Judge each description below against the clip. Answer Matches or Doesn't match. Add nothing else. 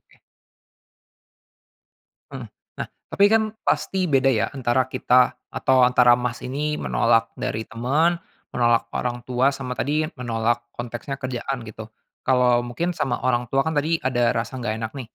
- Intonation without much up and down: Matches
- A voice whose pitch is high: Doesn't match